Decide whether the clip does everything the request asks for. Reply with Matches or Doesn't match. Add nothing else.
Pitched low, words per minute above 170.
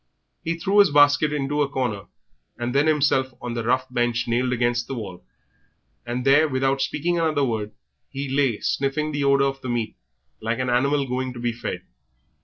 Matches